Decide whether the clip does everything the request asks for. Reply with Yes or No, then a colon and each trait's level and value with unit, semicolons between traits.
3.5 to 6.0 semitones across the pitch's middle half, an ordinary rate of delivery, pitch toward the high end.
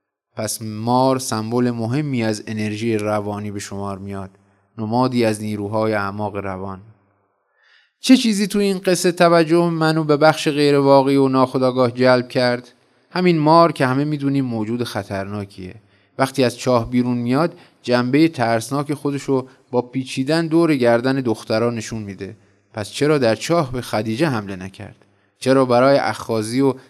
No: average, 4.7 semitones; average, 145 wpm; low, 125 Hz